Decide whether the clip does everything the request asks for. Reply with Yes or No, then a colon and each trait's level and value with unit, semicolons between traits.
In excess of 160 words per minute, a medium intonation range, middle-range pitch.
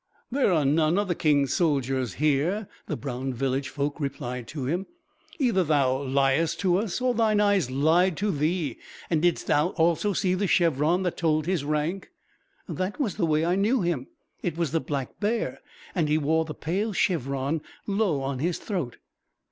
Yes: average, 180 wpm; average, 4.9 semitones; medium, 160 Hz